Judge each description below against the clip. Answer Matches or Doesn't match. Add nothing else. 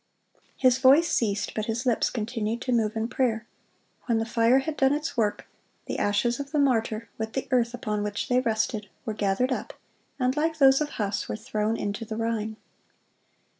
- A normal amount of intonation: Matches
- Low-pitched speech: Doesn't match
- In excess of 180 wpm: Matches